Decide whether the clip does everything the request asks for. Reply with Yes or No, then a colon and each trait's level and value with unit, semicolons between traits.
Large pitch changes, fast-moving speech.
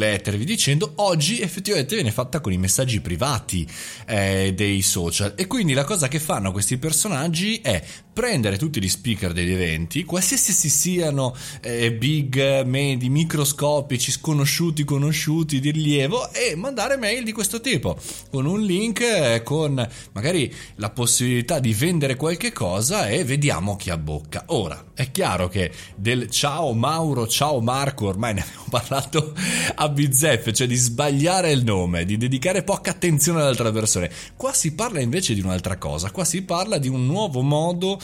No: wide, 6.8 semitones; average, 160 wpm